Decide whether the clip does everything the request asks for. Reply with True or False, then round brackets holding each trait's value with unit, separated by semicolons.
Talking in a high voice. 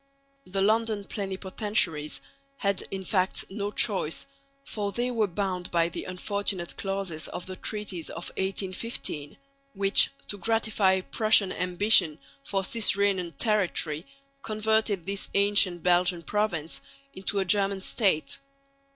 True (195 Hz)